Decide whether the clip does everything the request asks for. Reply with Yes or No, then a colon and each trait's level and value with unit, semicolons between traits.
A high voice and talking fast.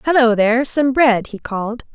No: high, 240 Hz; average, 185 wpm